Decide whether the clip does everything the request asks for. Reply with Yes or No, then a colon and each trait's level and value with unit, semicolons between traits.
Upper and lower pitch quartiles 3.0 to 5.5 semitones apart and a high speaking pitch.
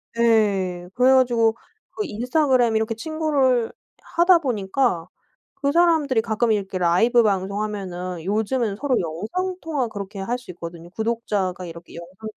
Yes: average, 5.2 semitones; high, 220 Hz